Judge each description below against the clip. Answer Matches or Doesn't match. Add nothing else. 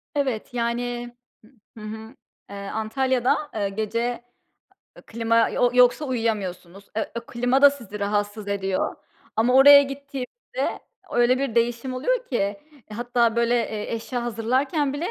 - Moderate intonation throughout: Matches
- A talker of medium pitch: Doesn't match